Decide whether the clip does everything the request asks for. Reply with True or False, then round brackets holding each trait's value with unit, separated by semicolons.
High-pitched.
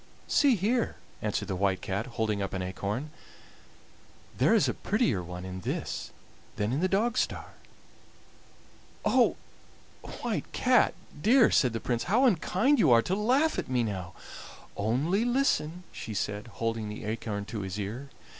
False (115 Hz)